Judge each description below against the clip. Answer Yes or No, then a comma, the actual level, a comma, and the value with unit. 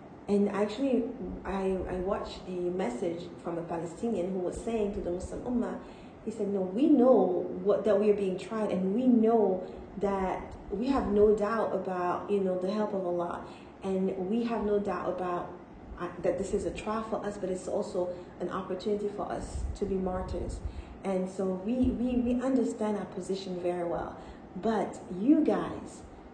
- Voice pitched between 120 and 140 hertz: No, high, 195 Hz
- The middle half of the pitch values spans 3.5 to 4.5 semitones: No, narrow, 2.6 semitones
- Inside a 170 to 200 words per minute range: Yes, average, 180 wpm